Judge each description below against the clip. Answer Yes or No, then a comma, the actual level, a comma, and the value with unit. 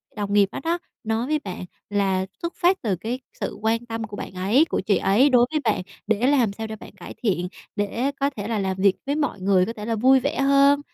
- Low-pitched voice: No, high, 225 Hz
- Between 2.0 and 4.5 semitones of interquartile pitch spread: No, average, 5.2 semitones